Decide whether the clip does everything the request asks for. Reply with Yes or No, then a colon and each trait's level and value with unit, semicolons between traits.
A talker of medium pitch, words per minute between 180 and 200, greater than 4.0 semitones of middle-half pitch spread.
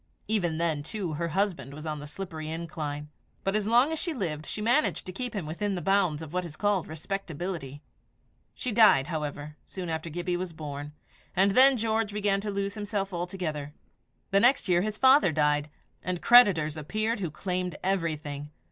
Yes: medium, 180 Hz; average, 185 wpm; average, 4.9 semitones